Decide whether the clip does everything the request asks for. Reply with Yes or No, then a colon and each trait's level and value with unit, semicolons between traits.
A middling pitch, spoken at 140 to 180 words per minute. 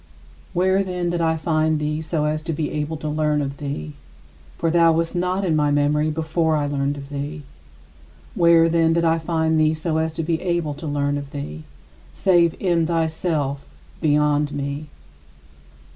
Yes: medium, 155 Hz; average, 175 wpm